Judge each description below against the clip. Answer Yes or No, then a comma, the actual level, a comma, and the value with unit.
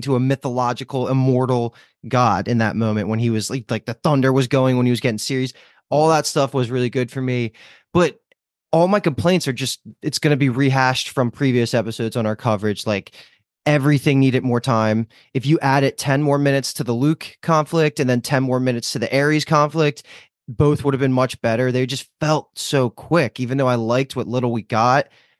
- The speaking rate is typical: No, fast, 215 wpm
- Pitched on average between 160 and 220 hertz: No, low, 130 Hz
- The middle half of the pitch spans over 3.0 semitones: No, average, 2.7 semitones